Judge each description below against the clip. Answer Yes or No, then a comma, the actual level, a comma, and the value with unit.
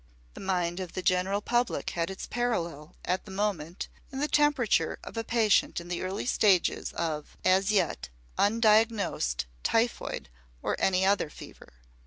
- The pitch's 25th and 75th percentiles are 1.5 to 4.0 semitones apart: No, average, 4.5 semitones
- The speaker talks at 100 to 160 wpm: Yes, average, 155 wpm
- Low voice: No, high, 190 Hz